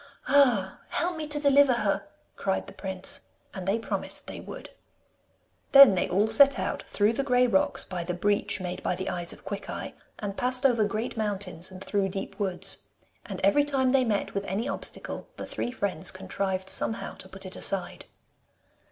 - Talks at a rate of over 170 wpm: Yes, average, 185 wpm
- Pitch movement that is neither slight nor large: Yes, average, 5.0 semitones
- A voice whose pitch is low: No, high, 205 Hz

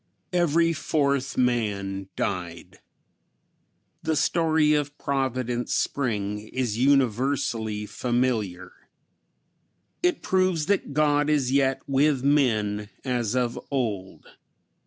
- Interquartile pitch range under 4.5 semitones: No, average, 5.2 semitones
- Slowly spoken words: Yes, slow, 95 wpm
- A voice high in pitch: No, low, 130 Hz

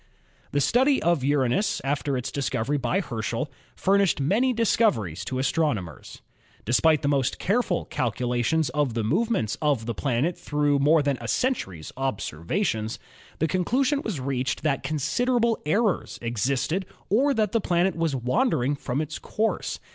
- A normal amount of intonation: No, wide, 7.5 semitones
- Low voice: No, medium, 145 Hz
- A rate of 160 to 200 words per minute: No, average, 150 wpm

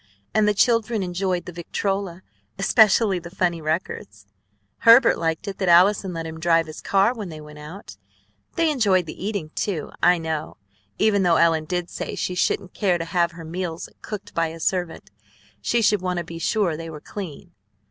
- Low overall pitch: No, medium, 180 Hz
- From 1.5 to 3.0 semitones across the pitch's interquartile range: No, average, 3.4 semitones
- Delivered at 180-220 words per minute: Yes, average, 190 wpm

